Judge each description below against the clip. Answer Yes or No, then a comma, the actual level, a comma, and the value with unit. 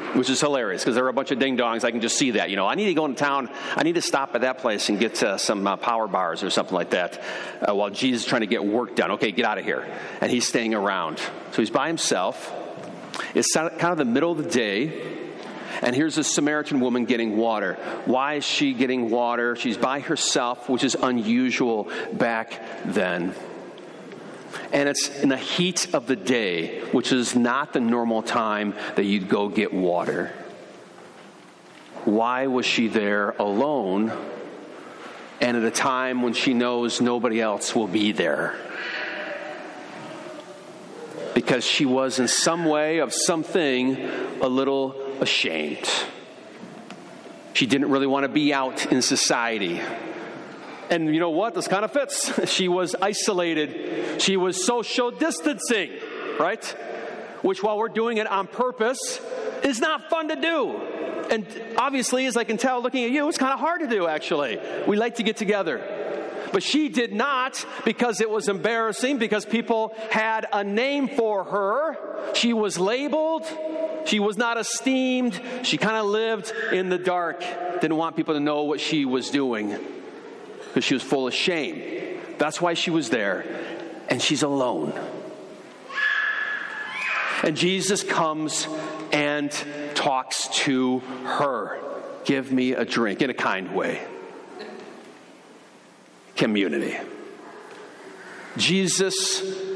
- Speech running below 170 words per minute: Yes, average, 160 wpm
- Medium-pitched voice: Yes, medium, 180 Hz